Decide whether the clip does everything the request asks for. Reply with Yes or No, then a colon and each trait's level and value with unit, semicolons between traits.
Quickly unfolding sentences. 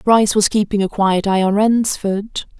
No: average, 185 wpm